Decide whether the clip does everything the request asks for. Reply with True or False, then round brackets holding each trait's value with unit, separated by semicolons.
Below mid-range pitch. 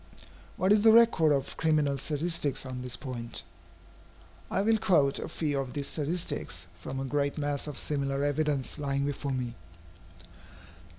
False (145 Hz)